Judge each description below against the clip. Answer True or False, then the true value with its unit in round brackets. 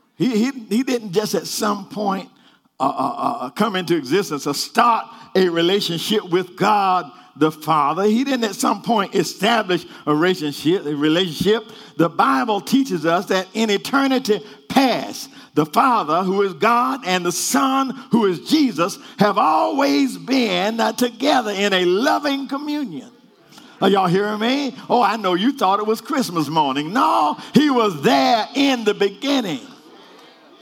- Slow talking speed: False (155 wpm)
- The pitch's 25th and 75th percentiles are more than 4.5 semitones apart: True (5.1 semitones)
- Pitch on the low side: False (215 Hz)